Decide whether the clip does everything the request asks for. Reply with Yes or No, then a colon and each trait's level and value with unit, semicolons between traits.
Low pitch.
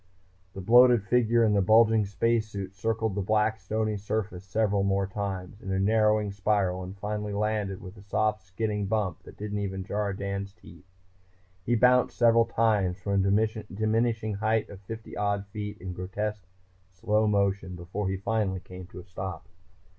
Yes: low, 105 Hz